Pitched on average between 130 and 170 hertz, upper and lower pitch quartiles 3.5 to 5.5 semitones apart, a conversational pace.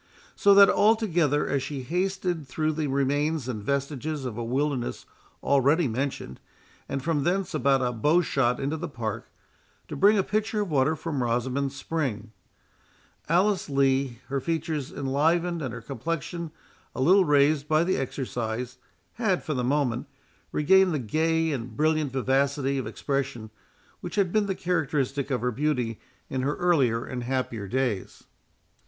Yes: medium, 140 Hz; average, 4.2 semitones; average, 155 wpm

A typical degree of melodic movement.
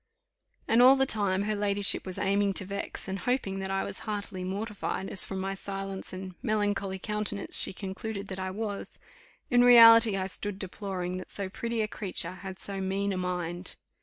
No: narrow, 1.9 semitones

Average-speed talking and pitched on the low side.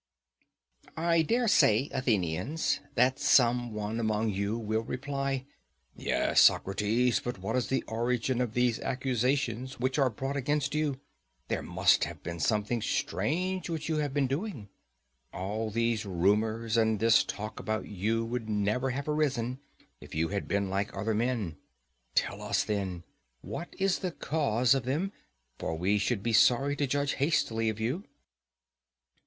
Yes: average, 155 wpm; low, 120 Hz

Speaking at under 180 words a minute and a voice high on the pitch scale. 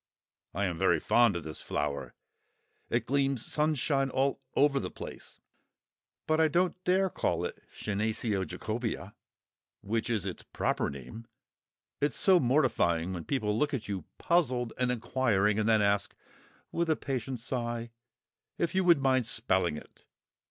No: average, 150 wpm; low, 120 Hz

